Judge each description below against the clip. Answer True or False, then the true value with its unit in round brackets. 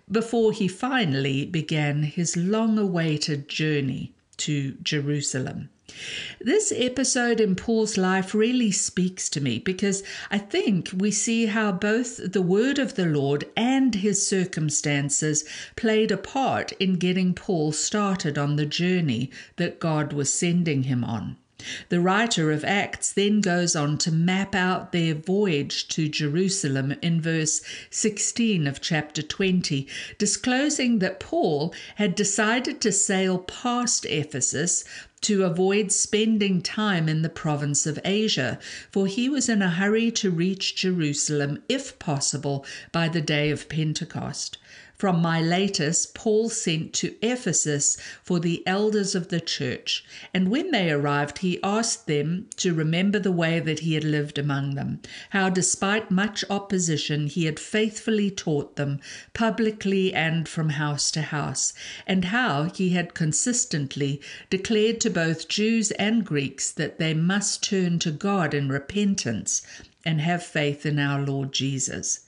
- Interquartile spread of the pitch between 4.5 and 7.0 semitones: True (5.6 semitones)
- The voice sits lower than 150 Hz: False (180 Hz)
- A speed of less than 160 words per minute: True (145 wpm)